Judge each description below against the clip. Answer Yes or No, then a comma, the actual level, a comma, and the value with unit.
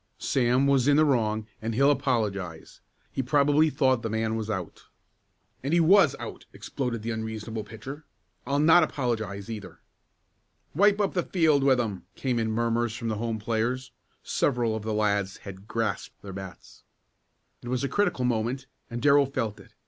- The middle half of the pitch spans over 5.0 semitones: No, average, 4.1 semitones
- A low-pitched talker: Yes, low, 120 Hz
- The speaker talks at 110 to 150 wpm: No, average, 170 wpm